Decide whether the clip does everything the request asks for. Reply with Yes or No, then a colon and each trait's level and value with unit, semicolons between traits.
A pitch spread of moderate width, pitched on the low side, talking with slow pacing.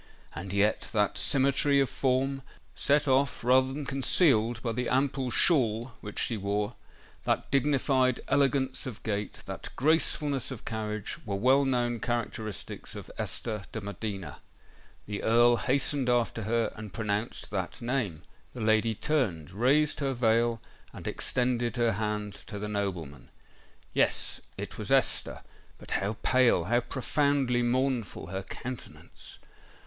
Yes: average, 3.9 semitones; low, 120 Hz; slow, 125 wpm